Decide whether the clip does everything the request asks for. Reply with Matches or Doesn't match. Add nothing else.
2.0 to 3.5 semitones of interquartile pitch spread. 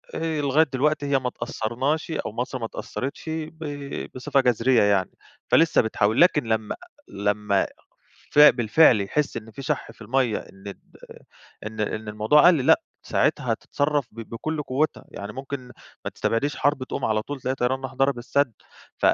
Doesn't match